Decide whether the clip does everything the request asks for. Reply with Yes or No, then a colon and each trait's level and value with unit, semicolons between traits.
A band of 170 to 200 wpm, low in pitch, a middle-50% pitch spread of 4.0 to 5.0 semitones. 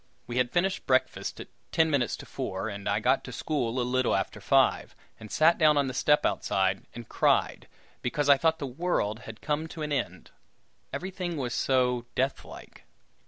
Yes: average, 190 wpm; low, 130 Hz; average, 4.5 semitones